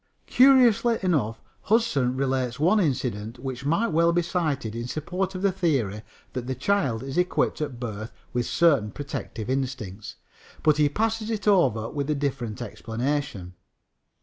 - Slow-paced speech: No, average, 150 wpm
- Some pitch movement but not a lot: No, wide, 6.9 semitones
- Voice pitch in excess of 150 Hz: No, medium, 140 Hz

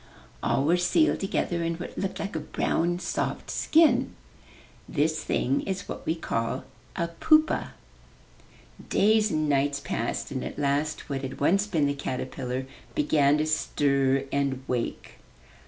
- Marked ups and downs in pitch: No, average, 4.1 semitones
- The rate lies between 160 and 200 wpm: No, average, 145 wpm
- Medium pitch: Yes, medium, 150 Hz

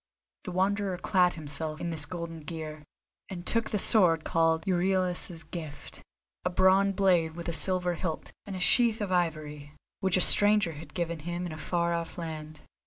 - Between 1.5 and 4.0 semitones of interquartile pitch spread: Yes, average, 2.7 semitones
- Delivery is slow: No, average, 175 wpm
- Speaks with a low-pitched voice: No, medium, 175 Hz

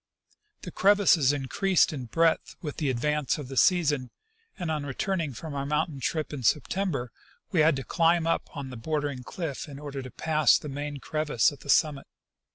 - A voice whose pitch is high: No, medium, 150 Hz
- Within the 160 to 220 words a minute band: Yes, average, 190 wpm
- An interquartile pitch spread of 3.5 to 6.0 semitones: No, average, 3.0 semitones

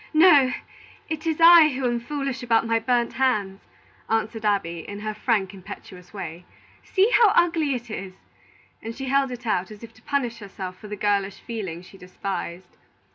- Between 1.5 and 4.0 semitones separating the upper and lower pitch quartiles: No, average, 5.3 semitones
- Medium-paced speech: Yes, average, 180 wpm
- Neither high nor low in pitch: No, high, 225 Hz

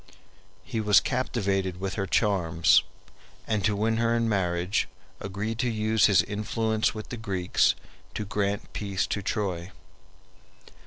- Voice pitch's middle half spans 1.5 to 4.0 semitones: Yes, narrow, 2.4 semitones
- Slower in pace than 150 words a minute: Yes, average, 140 wpm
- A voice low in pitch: Yes, low, 105 Hz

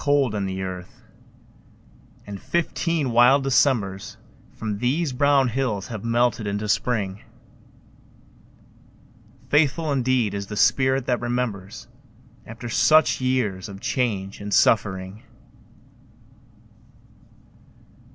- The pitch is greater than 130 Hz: No, low, 120 Hz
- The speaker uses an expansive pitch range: No, average, 4.7 semitones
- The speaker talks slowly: Yes, slow, 100 wpm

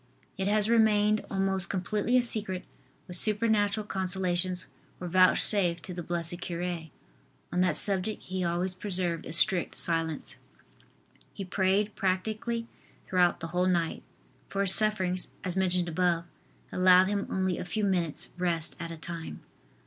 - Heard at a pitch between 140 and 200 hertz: Yes, medium, 185 Hz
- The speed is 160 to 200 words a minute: No, average, 145 wpm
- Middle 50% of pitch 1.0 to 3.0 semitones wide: Yes, narrow, 2.5 semitones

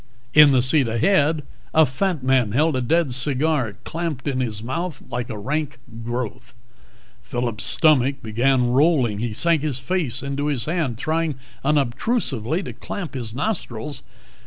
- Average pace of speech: Yes, average, 150 wpm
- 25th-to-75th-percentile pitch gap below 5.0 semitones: Yes, average, 4.5 semitones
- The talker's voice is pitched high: No, low, 135 Hz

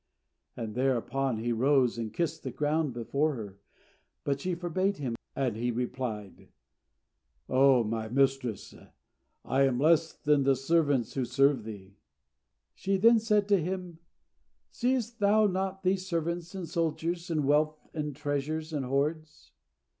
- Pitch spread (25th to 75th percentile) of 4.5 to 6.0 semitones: Yes, average, 5.2 semitones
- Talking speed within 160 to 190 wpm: No, average, 140 wpm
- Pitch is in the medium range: Yes, medium, 145 Hz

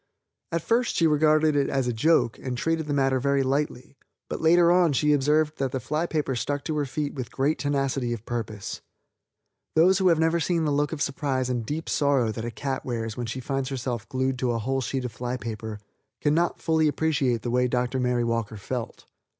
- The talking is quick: Yes, fast, 215 wpm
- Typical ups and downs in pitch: Yes, average, 3.8 semitones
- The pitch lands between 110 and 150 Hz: Yes, low, 135 Hz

